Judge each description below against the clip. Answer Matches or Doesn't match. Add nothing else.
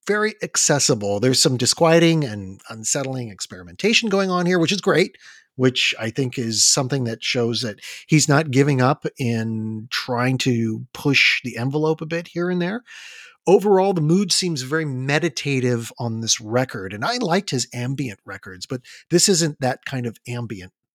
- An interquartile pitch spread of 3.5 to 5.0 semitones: Doesn't match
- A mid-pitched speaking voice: Doesn't match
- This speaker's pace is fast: Doesn't match